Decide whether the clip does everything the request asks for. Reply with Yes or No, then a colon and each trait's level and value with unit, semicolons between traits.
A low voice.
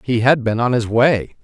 Yes: low, 120 Hz